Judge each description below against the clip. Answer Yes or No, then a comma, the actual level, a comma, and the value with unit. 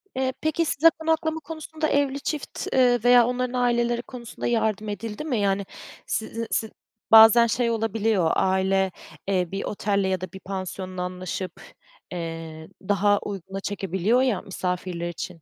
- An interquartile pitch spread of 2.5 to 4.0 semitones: No, average, 4.6 semitones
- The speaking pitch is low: No, high, 210 Hz